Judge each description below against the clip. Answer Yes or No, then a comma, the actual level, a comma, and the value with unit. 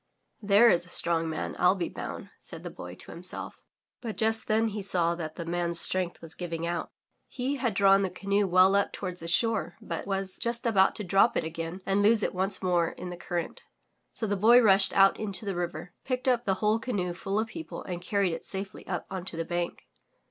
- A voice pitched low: No, high, 190 Hz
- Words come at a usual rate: No, fast, 235 wpm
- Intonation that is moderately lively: Yes, average, 3.3 semitones